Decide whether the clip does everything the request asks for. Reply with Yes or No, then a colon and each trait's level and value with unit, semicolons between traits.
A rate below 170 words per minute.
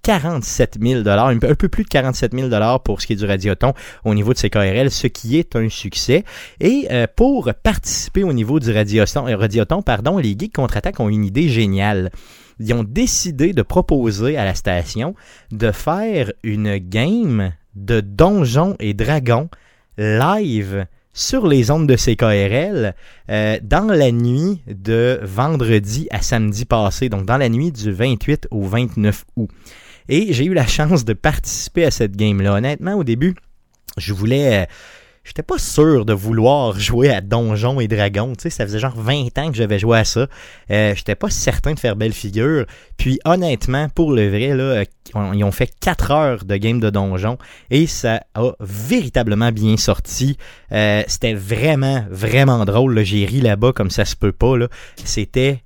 No: average, 175 wpm